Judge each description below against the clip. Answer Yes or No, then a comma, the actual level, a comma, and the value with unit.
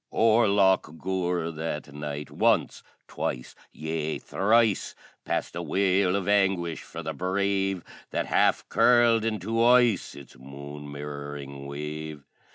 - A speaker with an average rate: No, slow, 125 wpm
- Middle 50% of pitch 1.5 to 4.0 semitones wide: No, average, 5.2 semitones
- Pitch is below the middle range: Yes, very low, 85 Hz